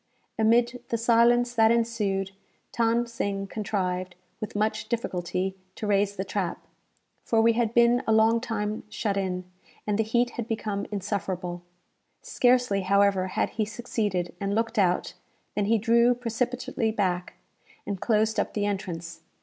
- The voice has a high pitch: Yes, high, 215 Hz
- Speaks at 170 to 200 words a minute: No, average, 150 wpm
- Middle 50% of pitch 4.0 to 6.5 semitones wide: No, average, 2.9 semitones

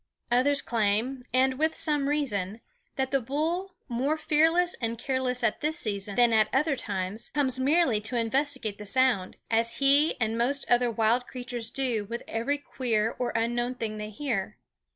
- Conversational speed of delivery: Yes, average, 170 wpm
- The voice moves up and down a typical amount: Yes, average, 3.9 semitones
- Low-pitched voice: No, high, 245 Hz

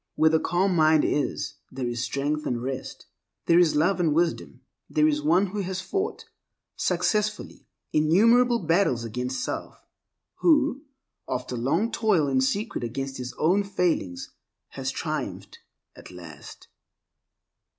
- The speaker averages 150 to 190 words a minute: No, slow, 135 wpm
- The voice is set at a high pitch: No, medium, 160 Hz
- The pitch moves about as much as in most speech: No, wide, 7.1 semitones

